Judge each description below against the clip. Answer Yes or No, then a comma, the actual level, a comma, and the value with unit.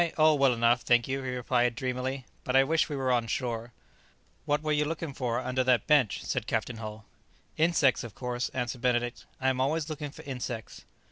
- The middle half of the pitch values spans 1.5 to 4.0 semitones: Yes, narrow, 2.5 semitones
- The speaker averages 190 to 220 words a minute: Yes, average, 200 wpm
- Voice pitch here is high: No, low, 130 Hz